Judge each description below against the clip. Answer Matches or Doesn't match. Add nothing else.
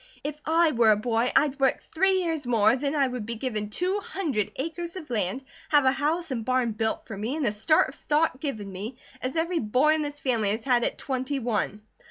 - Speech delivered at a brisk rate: Matches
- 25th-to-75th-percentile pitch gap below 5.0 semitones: Doesn't match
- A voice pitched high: Matches